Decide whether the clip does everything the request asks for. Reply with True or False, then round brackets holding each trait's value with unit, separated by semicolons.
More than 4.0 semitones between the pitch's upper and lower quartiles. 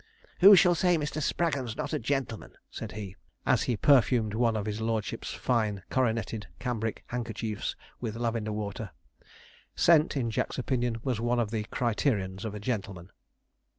False (3.1 semitones)